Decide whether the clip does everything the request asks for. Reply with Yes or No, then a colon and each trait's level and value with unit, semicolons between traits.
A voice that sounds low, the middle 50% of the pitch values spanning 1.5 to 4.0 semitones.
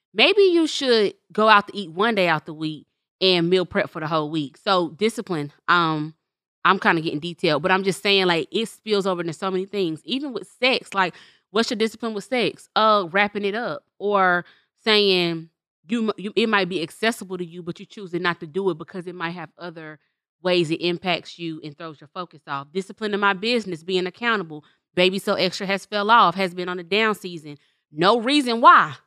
No: medium, 185 Hz; average, 3.6 semitones